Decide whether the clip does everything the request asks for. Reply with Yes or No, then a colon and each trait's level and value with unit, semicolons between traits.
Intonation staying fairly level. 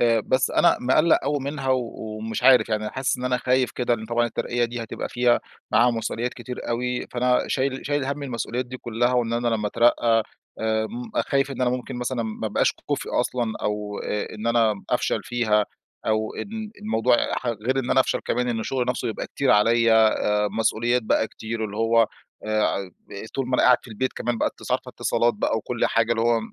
Yes: narrow, 2.3 semitones